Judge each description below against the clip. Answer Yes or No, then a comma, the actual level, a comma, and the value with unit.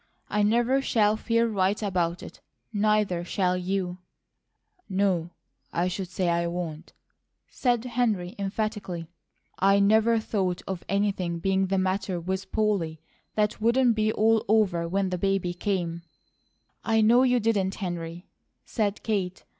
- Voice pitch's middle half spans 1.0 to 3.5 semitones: Yes, average, 3.2 semitones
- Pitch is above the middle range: Yes, high, 195 Hz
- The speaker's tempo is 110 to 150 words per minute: Yes, average, 145 wpm